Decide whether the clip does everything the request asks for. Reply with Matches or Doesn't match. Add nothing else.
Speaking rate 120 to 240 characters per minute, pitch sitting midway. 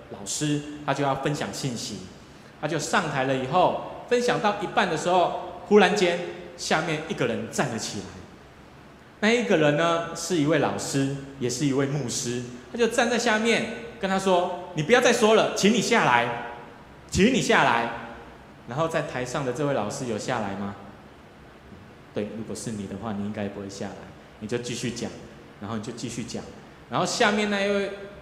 Doesn't match